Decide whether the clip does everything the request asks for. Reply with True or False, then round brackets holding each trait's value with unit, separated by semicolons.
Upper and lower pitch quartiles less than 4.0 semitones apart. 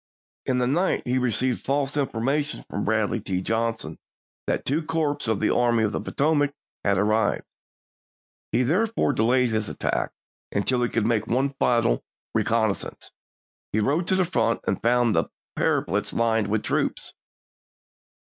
False (4.3 semitones)